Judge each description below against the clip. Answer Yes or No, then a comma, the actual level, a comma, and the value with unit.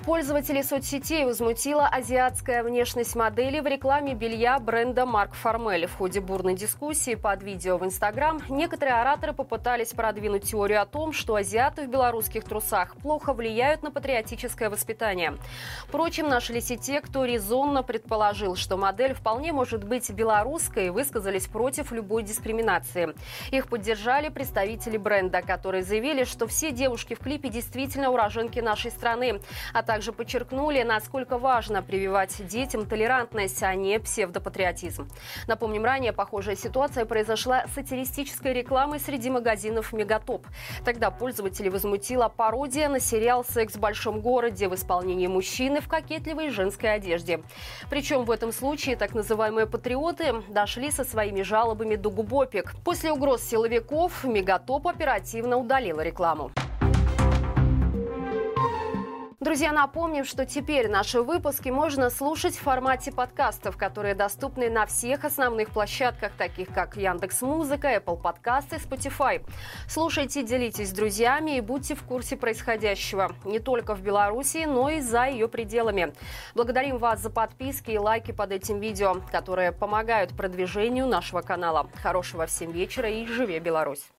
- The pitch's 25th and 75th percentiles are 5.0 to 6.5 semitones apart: No, average, 4.4 semitones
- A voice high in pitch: Yes, high, 230 Hz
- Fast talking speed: No, average, 135 wpm